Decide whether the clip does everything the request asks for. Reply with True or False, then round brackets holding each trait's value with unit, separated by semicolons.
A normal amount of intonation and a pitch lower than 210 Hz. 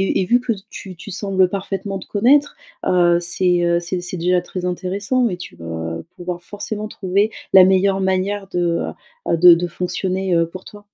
False (2.1 semitones; 185 Hz)